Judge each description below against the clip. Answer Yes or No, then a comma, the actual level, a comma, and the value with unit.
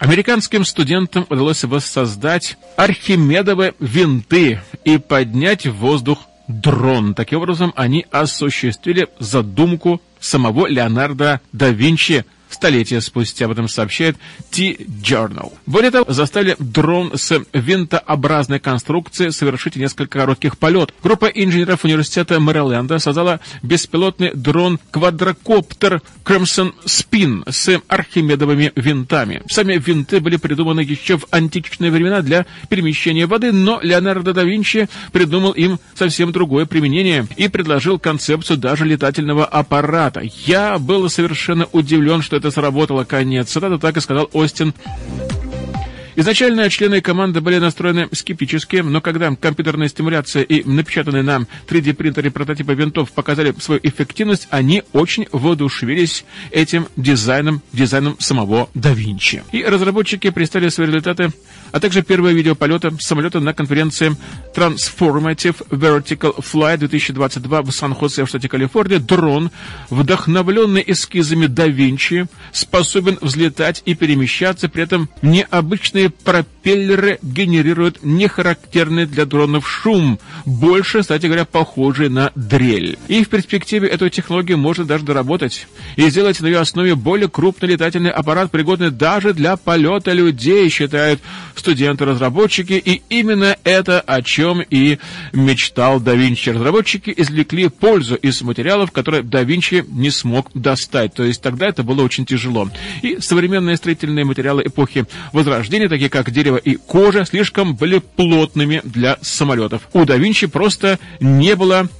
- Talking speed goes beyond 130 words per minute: No, average, 125 wpm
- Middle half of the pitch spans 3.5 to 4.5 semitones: Yes, average, 4.2 semitones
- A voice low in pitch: No, medium, 160 Hz